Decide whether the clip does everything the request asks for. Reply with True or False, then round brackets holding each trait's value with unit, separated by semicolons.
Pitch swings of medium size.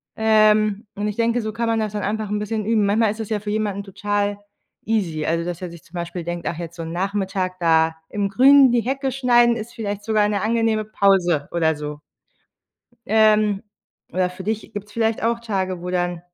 True (3.4 semitones)